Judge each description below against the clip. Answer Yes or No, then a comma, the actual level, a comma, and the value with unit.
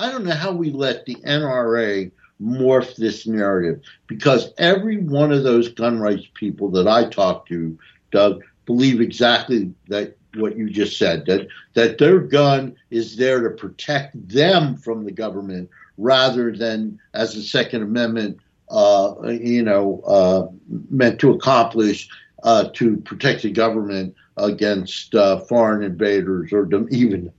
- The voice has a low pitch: Yes, low, 110 Hz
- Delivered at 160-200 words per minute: No, average, 145 wpm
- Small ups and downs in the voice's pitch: No, average, 3.7 semitones